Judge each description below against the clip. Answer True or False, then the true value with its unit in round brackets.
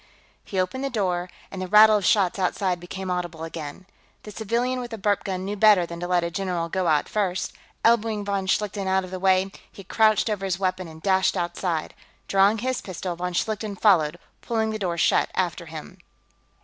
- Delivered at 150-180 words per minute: False (200 wpm)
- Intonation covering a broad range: False (3.0 semitones)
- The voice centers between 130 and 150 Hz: False (190 Hz)